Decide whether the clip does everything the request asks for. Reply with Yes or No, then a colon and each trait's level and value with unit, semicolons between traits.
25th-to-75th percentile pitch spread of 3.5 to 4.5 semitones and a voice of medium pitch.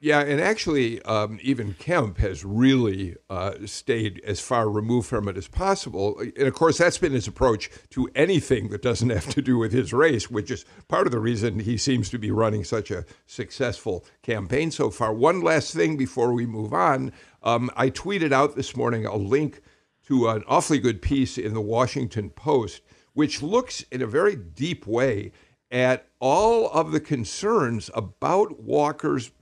No: average, 4.2 semitones; low, 120 Hz